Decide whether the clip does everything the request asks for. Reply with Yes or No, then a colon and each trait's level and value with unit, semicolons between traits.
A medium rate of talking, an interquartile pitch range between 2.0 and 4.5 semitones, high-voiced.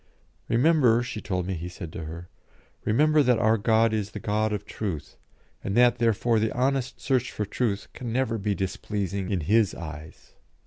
No: average, 180 wpm; average, 3.8 semitones; low, 110 Hz